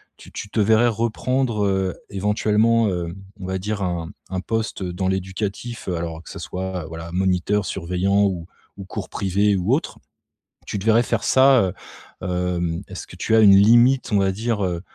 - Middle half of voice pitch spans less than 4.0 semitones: Yes, average, 3.3 semitones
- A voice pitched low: Yes, low, 100 Hz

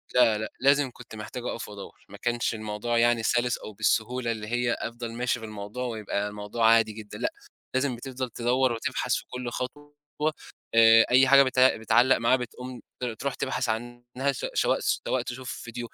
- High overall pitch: No, low, 120 Hz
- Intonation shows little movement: Yes, narrow, 2.1 semitones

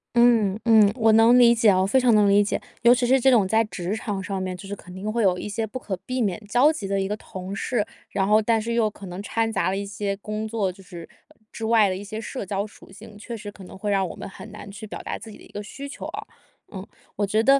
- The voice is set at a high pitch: Yes, high, 210 Hz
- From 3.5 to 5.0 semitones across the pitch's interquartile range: No, narrow, 2.5 semitones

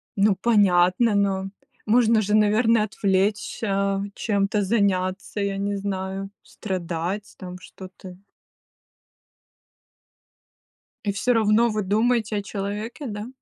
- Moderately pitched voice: No, high, 200 Hz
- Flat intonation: Yes, narrow, 2.0 semitones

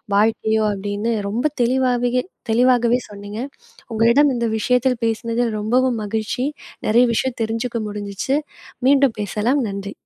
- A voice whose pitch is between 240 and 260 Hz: No, high, 230 Hz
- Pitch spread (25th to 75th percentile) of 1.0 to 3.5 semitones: Yes, average, 2.8 semitones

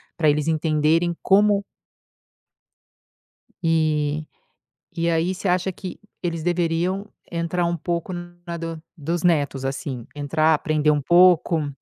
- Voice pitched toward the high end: No, medium, 165 Hz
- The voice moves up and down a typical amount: No, narrow, 2.3 semitones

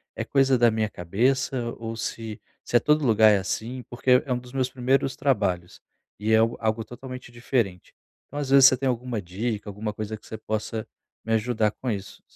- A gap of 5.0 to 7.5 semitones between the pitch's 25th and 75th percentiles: No, average, 3.0 semitones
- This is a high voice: No, low, 115 Hz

